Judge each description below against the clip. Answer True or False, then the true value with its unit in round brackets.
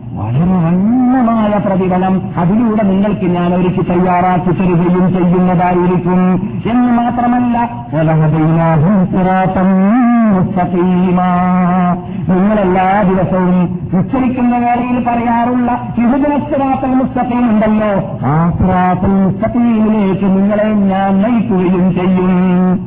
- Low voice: False (185 Hz)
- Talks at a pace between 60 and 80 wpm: True (70 wpm)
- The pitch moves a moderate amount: True (3.7 semitones)